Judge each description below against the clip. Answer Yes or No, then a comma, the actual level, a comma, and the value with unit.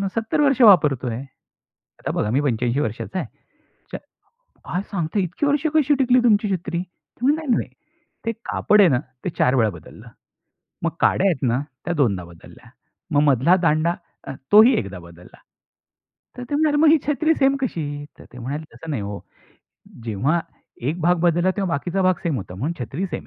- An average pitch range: No, wide, 8.8 semitones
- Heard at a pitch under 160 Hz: No, medium, 170 Hz